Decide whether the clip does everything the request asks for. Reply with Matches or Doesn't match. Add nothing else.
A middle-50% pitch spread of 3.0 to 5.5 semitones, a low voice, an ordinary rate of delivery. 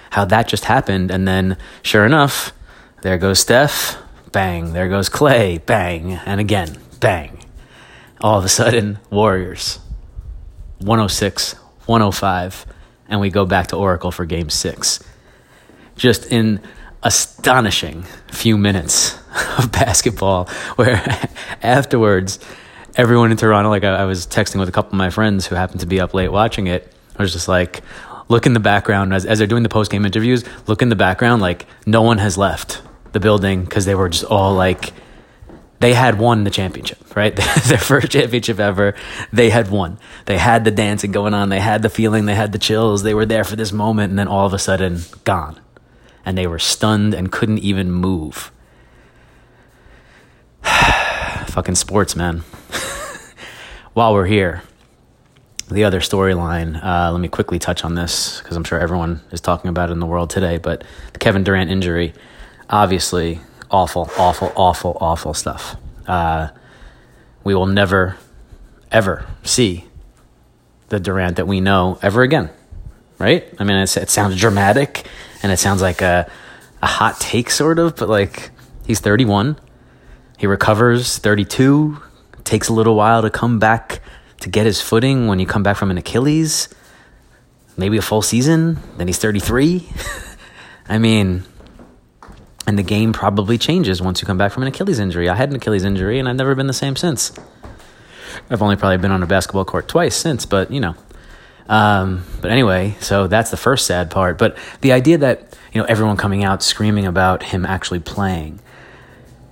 Matches